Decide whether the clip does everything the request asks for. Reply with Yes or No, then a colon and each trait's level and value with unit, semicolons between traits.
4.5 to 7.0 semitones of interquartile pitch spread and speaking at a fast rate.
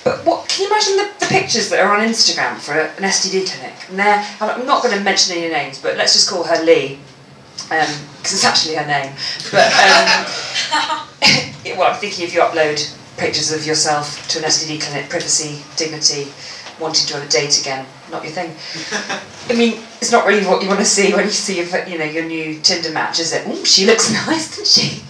Yes: average, 4.8 semitones; fast, 220 wpm